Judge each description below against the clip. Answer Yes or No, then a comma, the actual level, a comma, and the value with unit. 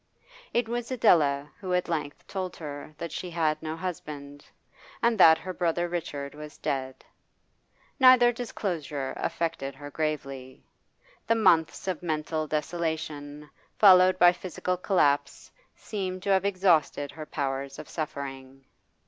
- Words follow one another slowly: Yes, slow, 130 wpm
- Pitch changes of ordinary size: Yes, average, 4.2 semitones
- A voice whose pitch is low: No, medium, 160 Hz